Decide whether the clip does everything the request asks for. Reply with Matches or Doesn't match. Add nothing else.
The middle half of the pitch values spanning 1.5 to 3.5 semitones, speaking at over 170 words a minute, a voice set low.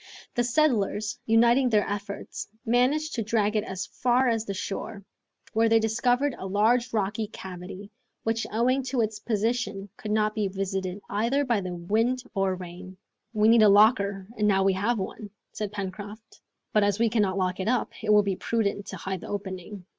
Doesn't match